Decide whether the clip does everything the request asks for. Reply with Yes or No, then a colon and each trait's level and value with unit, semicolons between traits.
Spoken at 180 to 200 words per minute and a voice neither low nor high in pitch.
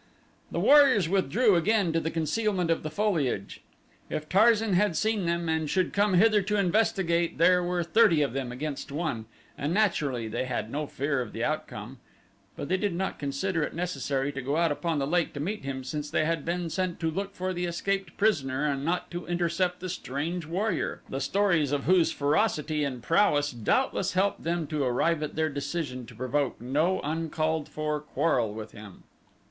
Yes: average, 190 wpm; medium, 165 Hz